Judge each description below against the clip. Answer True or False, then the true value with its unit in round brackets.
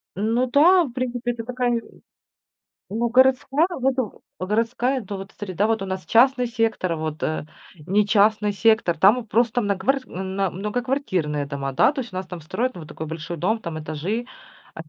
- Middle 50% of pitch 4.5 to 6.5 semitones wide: True (5.0 semitones)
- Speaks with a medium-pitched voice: False (215 Hz)